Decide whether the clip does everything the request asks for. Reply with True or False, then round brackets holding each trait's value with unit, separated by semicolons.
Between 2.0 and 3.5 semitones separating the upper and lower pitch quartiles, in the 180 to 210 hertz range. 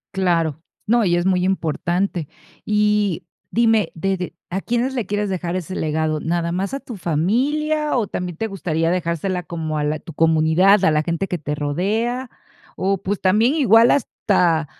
False (4.2 semitones; 185 Hz)